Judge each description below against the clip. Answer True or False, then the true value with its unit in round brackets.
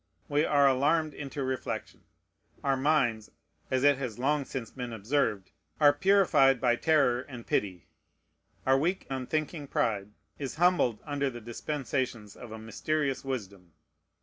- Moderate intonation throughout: True (3.7 semitones)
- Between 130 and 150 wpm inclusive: True (140 wpm)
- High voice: False (135 Hz)